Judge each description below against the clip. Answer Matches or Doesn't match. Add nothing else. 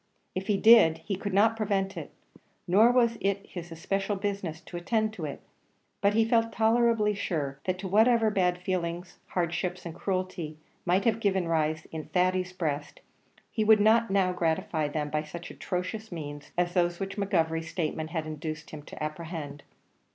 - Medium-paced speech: Matches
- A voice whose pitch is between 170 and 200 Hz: Matches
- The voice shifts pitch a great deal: Doesn't match